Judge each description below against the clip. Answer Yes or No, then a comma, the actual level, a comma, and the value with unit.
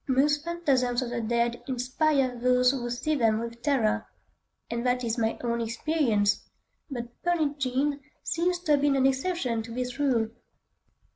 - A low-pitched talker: No, very high, 250 Hz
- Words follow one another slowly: No, average, 150 wpm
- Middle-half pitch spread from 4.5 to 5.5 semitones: No, average, 3.5 semitones